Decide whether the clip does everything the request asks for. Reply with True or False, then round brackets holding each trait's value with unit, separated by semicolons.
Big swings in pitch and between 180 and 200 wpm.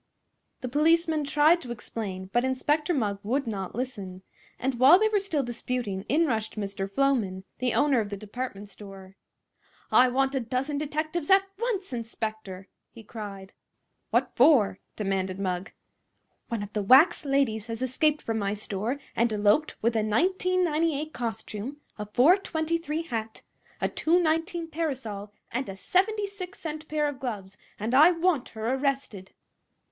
False (6.6 semitones; 150 wpm)